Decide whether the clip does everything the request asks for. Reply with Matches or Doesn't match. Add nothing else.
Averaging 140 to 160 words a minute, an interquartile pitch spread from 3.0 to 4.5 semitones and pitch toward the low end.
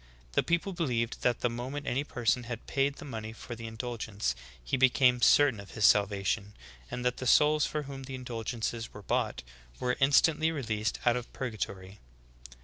Doesn't match